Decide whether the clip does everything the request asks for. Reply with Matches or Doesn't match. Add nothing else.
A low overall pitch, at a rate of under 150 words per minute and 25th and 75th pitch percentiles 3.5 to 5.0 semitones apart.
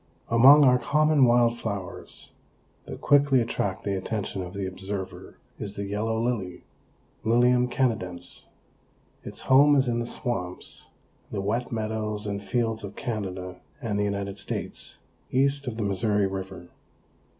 Matches